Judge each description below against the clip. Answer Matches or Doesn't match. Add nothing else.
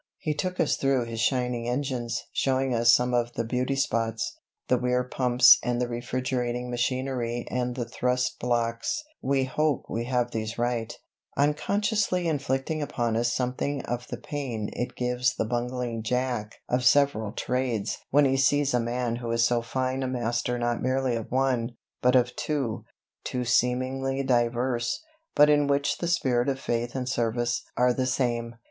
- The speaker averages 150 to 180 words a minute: Matches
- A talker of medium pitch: Doesn't match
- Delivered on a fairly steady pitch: Matches